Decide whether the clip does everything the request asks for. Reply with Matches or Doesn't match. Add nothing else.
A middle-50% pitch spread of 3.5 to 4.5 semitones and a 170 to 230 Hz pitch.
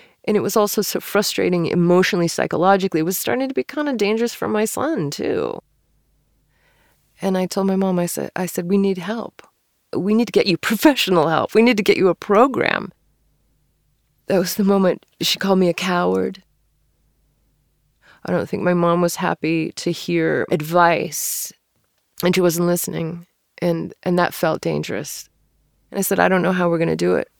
Doesn't match